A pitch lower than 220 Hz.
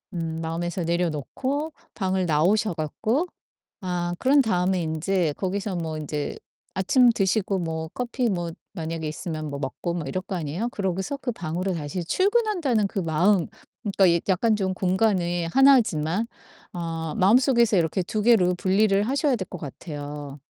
Yes: medium, 185 Hz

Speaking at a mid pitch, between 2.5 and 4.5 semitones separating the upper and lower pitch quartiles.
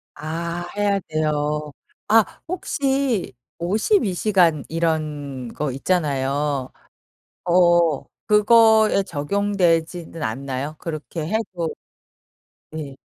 No: medium, 165 Hz; average, 5.2 semitones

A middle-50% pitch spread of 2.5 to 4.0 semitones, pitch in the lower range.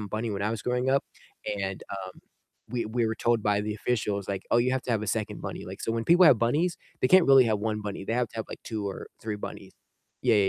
Yes: average, 3.1 semitones; low, 110 Hz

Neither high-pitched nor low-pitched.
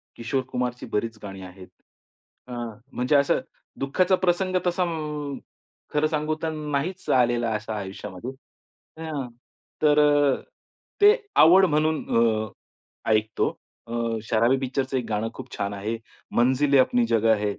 No: low, 130 Hz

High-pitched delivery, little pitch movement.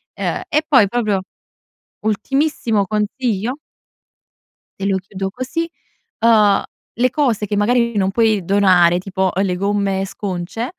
No: high, 205 Hz; average, 3.5 semitones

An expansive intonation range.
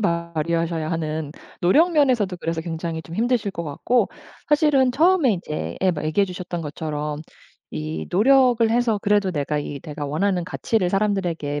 Yes: wide, 6.2 semitones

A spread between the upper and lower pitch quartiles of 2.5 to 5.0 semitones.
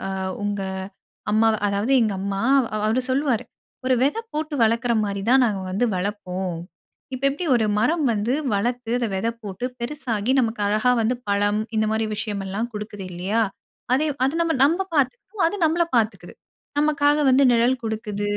Yes: average, 4.2 semitones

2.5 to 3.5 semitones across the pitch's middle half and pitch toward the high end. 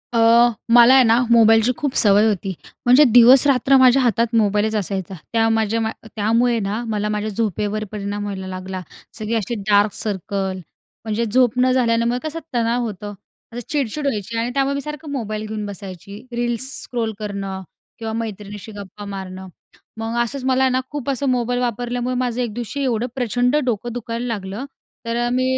Yes: average, 3.0 semitones; high, 230 Hz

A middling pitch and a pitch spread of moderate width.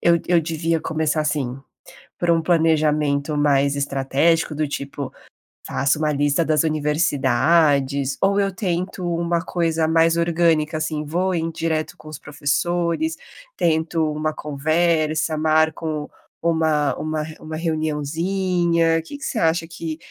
No: medium, 160 Hz; narrow, 2.0 semitones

